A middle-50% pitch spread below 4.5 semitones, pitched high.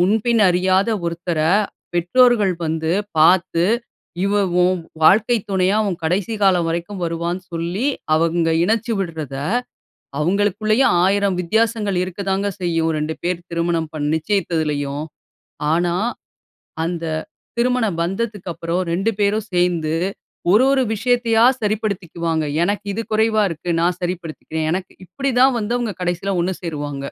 No: average, 3.8 semitones; medium, 180 Hz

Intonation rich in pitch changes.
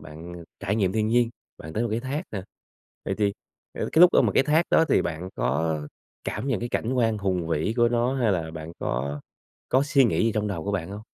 Yes: wide, 6.2 semitones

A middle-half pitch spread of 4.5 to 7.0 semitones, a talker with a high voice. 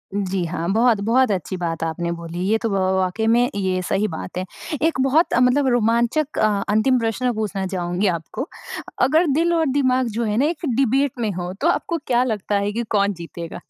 Yes: wide, 5.4 semitones; high, 220 Hz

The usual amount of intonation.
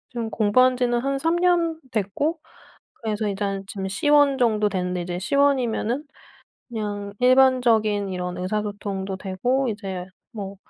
Yes: average, 4.6 semitones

